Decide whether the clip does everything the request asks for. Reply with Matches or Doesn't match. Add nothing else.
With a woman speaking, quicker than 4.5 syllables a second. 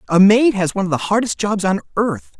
Doesn't match